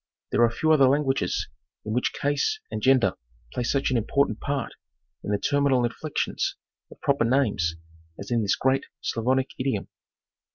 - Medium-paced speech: Yes, average, 160 wpm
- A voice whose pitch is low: Yes, low, 130 Hz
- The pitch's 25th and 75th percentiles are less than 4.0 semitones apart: Yes, average, 3.1 semitones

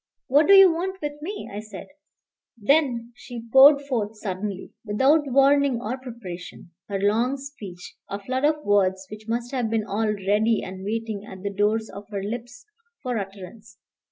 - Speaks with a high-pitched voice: Yes, high, 225 Hz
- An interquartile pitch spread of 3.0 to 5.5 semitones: Yes, average, 4.7 semitones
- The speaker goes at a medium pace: Yes, average, 170 wpm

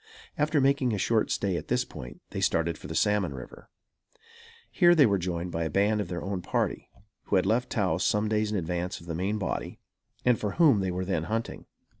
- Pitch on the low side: Yes, low, 100 Hz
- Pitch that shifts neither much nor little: Yes, average, 3.9 semitones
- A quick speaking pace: Yes, fast, 220 wpm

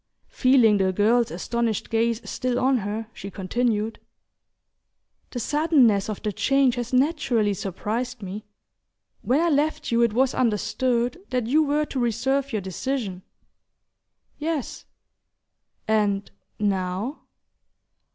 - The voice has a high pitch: Yes, high, 235 Hz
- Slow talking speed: Yes, slow, 120 wpm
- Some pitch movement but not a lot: Yes, average, 4.2 semitones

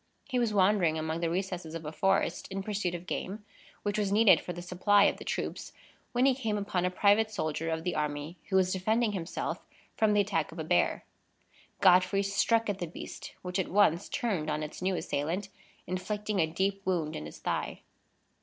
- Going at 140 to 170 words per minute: No, average, 200 wpm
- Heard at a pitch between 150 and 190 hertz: Yes, medium, 185 Hz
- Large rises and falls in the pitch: No, average, 3.7 semitones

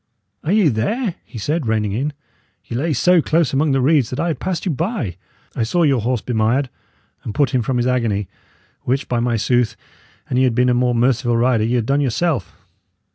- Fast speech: Yes, fast, 215 wpm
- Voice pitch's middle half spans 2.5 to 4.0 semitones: No, average, 4.4 semitones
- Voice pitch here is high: No, low, 125 Hz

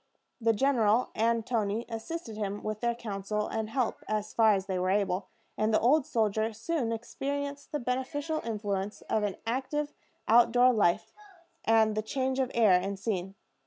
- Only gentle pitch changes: No, average, 3.3 semitones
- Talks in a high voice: Yes, high, 225 Hz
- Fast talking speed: No, average, 170 wpm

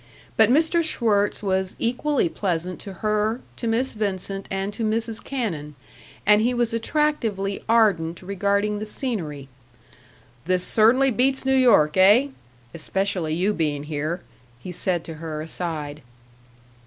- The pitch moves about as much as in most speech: Yes, average, 5.0 semitones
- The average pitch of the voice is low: No, high, 200 Hz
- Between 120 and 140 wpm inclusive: Yes, slow, 135 wpm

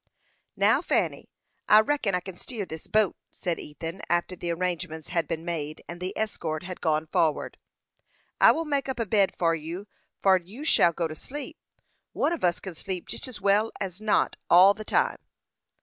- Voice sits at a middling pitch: Yes, medium, 180 Hz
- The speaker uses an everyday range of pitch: Yes, average, 4.3 semitones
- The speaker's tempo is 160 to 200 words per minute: Yes, average, 195 wpm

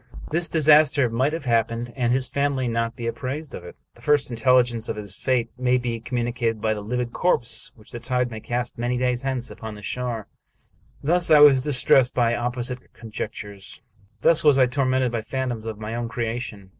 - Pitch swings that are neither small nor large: No, narrow, 2.3 semitones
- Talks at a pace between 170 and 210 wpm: Yes, average, 195 wpm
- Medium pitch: No, low, 125 Hz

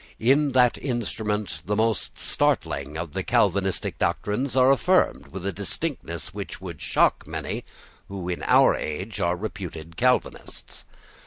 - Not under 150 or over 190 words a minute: No, average, 140 wpm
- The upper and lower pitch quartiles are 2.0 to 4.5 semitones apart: No, wide, 5.5 semitones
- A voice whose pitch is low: Yes, low, 100 Hz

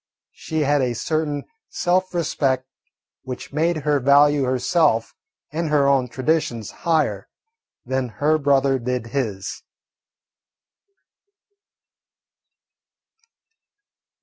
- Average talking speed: No, slow, 90 wpm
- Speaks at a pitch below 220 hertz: Yes, medium, 140 Hz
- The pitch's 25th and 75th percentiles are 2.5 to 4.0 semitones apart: Yes, average, 3.5 semitones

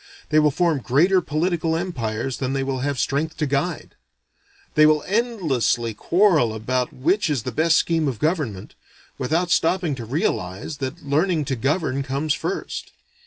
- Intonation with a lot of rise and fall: No, average, 4.2 semitones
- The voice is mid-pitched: Yes, medium, 150 Hz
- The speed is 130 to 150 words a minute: No, average, 160 wpm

